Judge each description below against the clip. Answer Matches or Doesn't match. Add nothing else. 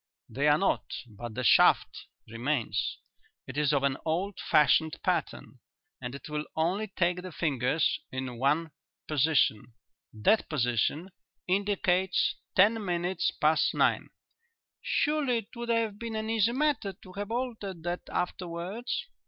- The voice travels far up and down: Matches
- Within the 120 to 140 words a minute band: Matches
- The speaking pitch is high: Doesn't match